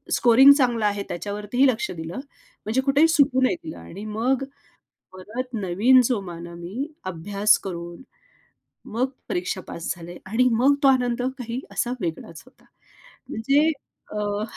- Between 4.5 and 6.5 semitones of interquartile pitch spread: Yes, wide, 5.5 semitones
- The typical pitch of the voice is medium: No, high, 225 Hz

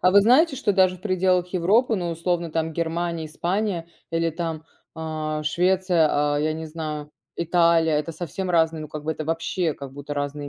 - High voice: No, medium, 165 Hz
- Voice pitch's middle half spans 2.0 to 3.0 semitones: Yes, average, 2.7 semitones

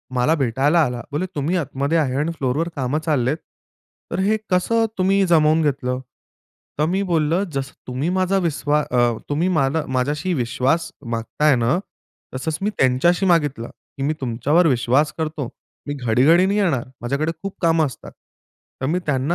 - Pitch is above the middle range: No, medium, 150 Hz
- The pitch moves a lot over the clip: No, average, 4.3 semitones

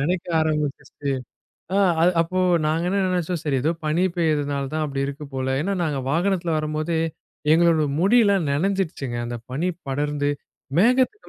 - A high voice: No, medium, 155 Hz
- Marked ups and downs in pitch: No, average, 3.7 semitones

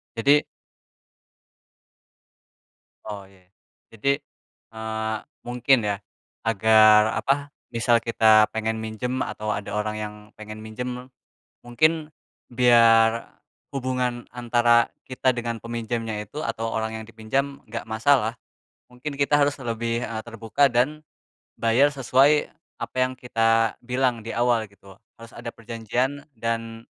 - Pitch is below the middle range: Yes, low, 115 Hz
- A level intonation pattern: Yes, narrow, 2.2 semitones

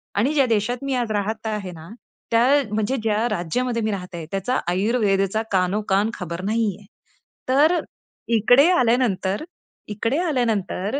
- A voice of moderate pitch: No, high, 215 Hz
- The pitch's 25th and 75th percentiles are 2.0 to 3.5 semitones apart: No, average, 4.0 semitones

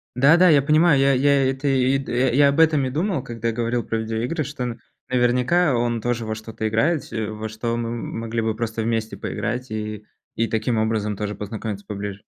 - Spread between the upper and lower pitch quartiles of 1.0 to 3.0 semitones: No, average, 3.6 semitones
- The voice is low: Yes, low, 120 Hz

